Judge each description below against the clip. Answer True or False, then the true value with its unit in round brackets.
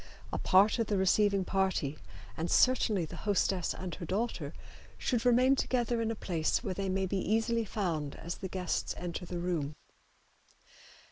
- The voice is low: False (190 Hz)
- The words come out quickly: False (165 wpm)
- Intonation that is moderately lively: True (4.1 semitones)